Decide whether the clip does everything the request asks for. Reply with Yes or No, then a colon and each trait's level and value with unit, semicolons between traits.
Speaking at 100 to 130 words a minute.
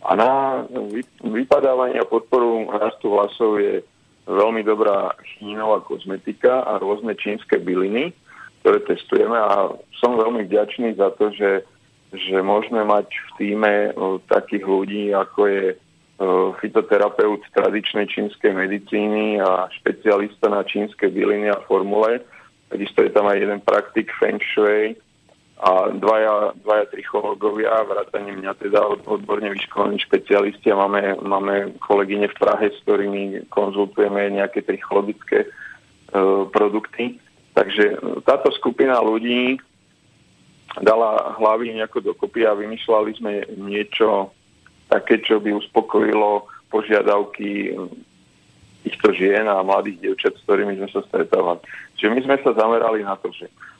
Yes: average, 125 wpm